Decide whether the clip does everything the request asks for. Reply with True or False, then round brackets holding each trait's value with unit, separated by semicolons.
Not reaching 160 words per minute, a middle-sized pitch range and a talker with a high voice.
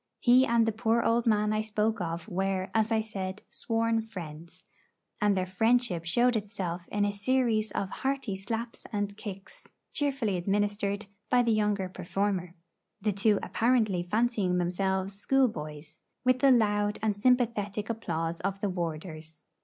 True (150 wpm; 3.4 semitones; 205 Hz)